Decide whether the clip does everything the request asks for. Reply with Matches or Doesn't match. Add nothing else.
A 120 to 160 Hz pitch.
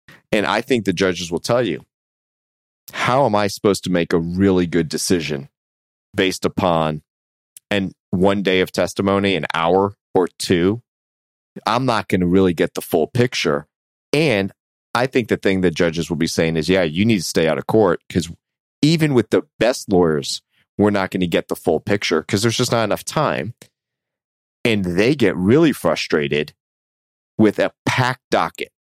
Doesn't match